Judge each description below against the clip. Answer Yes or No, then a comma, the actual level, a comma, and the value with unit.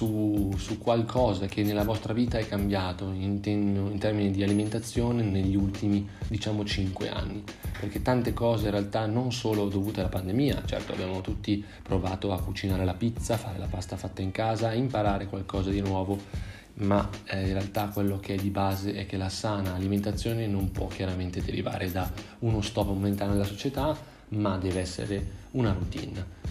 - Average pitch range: No, narrow, 1.9 semitones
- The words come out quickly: Yes, fast, 175 wpm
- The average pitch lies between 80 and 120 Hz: Yes, low, 100 Hz